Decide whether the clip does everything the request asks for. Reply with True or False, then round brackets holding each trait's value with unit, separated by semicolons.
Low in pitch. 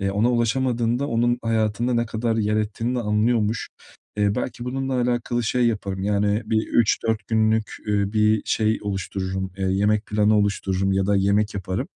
True (110 Hz)